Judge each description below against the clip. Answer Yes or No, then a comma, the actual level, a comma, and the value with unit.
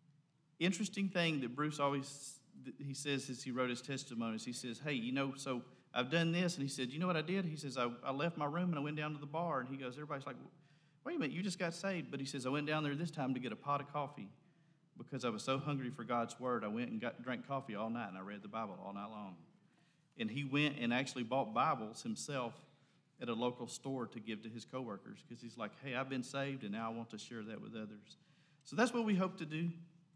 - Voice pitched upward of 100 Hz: Yes, medium, 140 Hz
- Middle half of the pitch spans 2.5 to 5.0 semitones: Yes, average, 4.4 semitones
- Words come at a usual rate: No, fast, 265 wpm